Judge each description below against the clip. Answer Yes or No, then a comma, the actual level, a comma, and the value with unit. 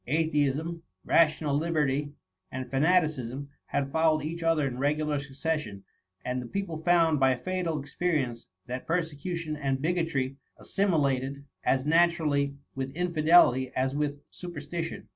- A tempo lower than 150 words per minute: Yes, average, 140 wpm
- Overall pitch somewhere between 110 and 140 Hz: No, medium, 150 Hz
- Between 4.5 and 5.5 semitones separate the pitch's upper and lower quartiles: No, average, 3.4 semitones